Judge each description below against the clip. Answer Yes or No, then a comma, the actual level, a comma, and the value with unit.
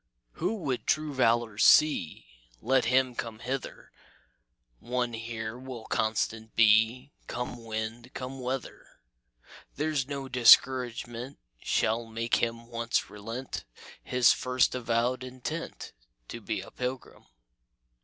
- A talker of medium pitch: No, low, 120 Hz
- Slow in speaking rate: Yes, slow, 115 wpm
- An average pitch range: No, narrow, 2.1 semitones